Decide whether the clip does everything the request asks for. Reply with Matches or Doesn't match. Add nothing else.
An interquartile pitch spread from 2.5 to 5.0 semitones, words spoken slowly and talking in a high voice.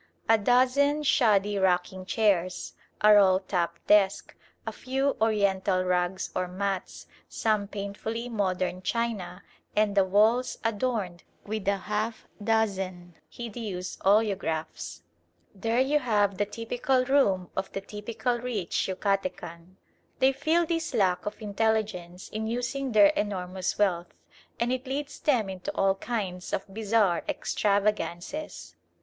Matches